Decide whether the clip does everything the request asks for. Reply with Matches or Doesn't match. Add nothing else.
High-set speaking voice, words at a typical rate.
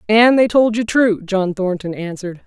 Matches